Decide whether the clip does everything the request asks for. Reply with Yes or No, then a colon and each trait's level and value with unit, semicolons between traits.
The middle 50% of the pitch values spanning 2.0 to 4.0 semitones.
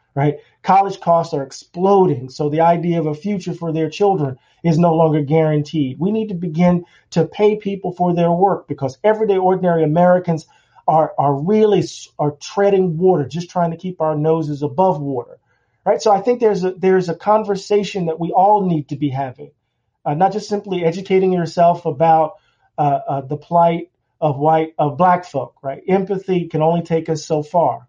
Yes: average, 3.6 semitones